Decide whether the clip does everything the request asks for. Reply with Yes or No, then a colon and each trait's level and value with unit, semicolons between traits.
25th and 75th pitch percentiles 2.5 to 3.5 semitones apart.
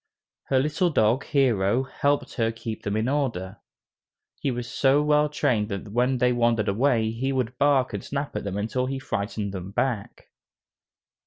No: average, 4.1 semitones